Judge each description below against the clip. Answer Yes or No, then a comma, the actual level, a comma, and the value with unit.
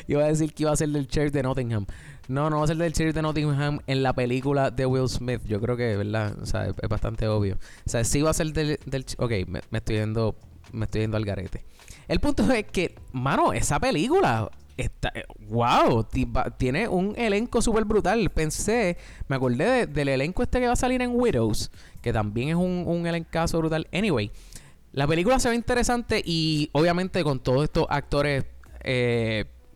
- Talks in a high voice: No, low, 135 Hz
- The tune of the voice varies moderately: No, wide, 6.9 semitones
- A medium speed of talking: No, fast, 205 wpm